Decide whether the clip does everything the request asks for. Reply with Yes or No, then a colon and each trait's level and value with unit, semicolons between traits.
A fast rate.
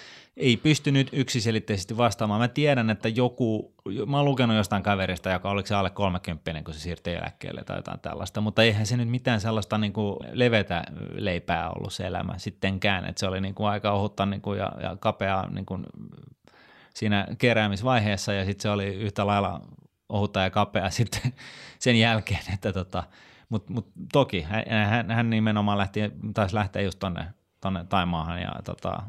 Yes: fast, 165 wpm